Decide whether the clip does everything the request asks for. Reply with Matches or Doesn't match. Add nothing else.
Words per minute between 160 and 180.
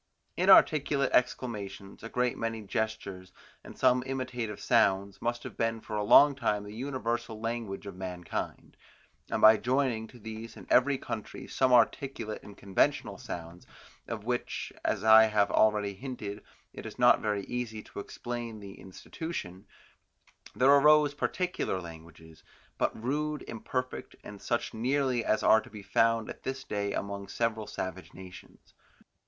Doesn't match